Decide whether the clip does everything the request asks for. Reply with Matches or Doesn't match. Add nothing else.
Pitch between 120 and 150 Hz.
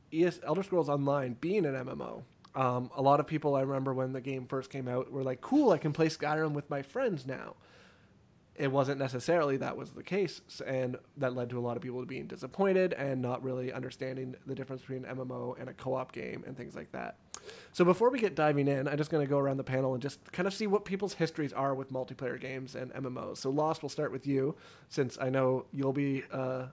Matches